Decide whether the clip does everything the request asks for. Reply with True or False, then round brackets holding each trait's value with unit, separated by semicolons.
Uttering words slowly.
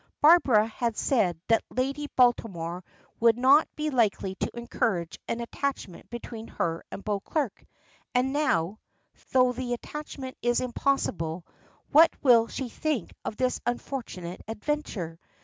True (130 wpm)